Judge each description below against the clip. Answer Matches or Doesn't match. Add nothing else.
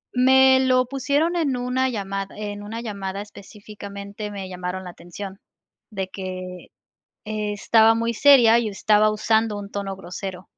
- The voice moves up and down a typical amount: Matches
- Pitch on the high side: Matches